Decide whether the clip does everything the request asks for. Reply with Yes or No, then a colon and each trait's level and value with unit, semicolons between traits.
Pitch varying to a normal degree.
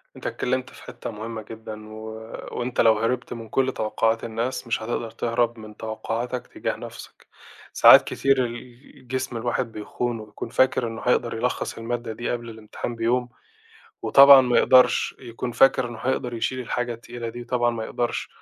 No: narrow, 1.7 semitones